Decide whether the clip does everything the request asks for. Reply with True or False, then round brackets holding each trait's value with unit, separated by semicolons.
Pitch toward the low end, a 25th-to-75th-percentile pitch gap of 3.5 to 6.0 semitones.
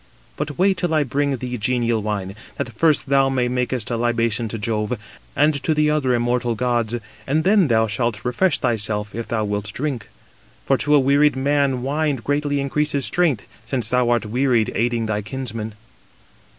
True (125 Hz; 3.9 semitones)